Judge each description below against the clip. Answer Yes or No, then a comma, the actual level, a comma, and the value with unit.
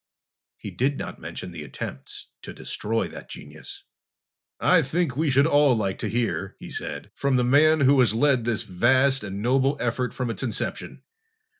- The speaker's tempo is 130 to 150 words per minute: No, average, 175 wpm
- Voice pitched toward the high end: No, low, 125 Hz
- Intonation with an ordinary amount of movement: Yes, average, 3.8 semitones